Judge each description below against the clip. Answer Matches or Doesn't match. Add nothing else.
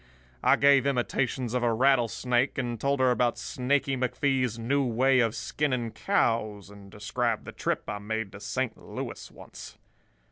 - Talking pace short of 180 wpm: Matches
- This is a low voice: Matches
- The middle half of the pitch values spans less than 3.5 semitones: Matches